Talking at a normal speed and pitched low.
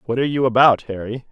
No: fast, 230 wpm; low, 125 Hz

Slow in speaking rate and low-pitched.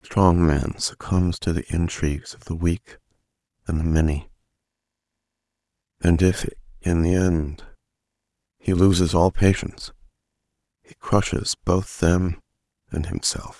Yes: slow, 125 wpm; very low, 85 Hz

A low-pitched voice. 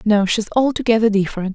No: high, 215 Hz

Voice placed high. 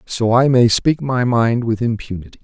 No: low, 120 Hz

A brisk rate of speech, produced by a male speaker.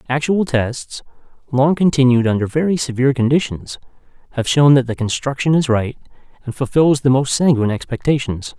No: average, 145 wpm; male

